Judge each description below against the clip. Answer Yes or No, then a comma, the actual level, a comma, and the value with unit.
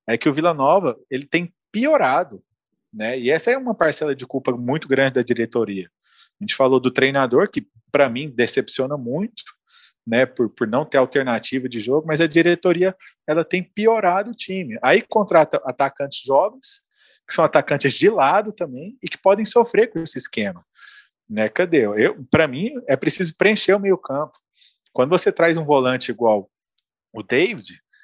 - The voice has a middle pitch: Yes, medium, 160 Hz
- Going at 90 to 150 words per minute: No, average, 175 wpm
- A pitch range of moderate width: No, wide, 7.8 semitones